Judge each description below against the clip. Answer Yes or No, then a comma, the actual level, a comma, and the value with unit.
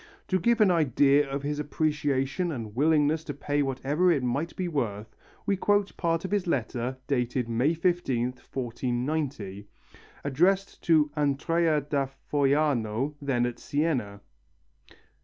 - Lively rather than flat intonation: No, average, 4.2 semitones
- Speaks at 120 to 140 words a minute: Yes, slow, 135 wpm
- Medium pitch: Yes, medium, 145 Hz